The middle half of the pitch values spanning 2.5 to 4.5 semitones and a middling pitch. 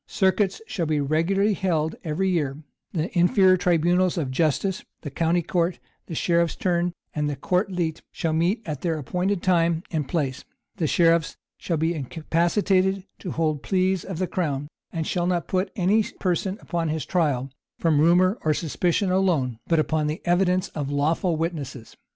Yes: average, 2.9 semitones; medium, 170 Hz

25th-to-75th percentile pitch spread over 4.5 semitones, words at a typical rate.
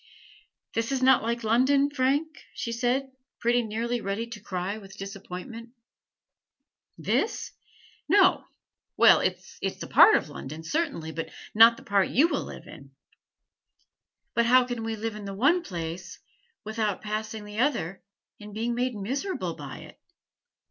No: average, 4.2 semitones; average, 155 wpm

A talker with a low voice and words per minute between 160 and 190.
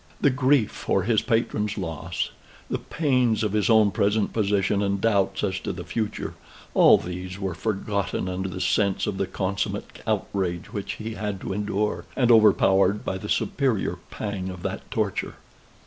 Yes: low, 100 Hz; average, 165 wpm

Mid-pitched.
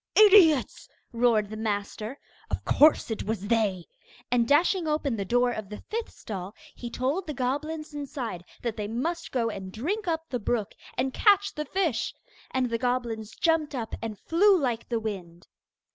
No: high, 245 Hz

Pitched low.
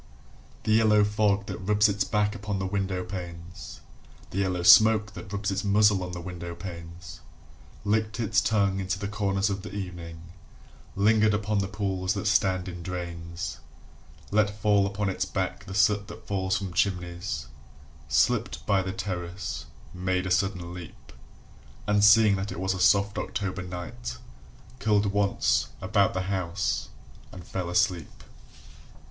Yes: very low, 95 Hz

